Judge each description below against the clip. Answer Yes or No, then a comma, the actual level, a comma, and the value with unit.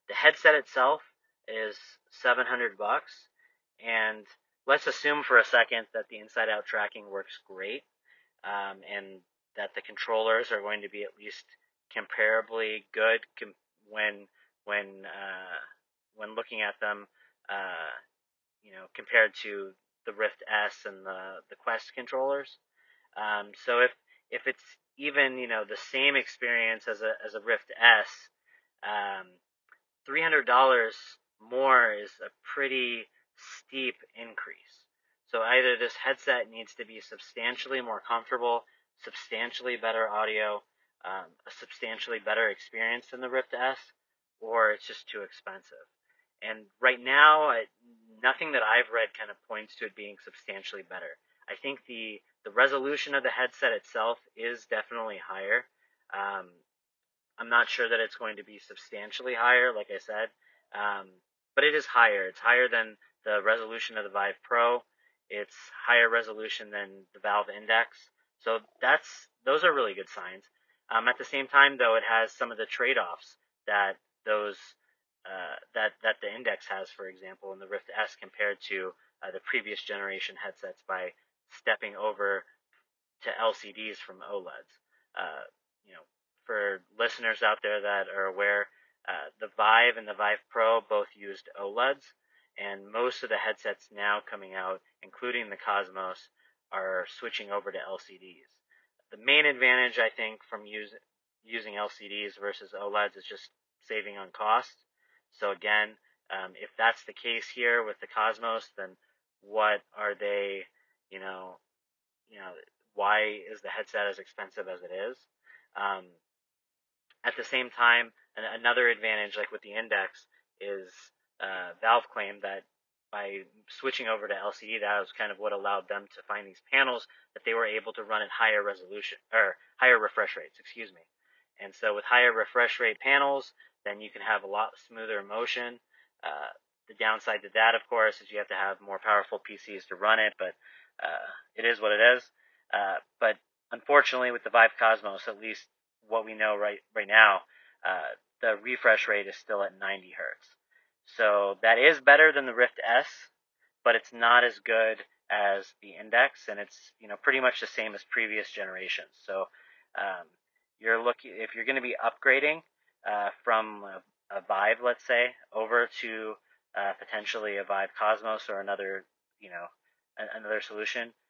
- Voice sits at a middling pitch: No, low, 115 Hz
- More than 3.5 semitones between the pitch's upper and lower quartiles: Yes, average, 5.1 semitones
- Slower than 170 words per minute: Yes, average, 160 wpm